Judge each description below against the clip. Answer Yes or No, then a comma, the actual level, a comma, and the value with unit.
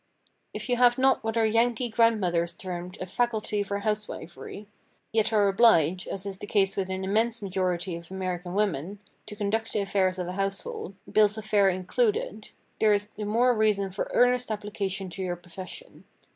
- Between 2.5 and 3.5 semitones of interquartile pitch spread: Yes, average, 2.9 semitones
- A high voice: Yes, high, 205 Hz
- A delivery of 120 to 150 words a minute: No, average, 170 wpm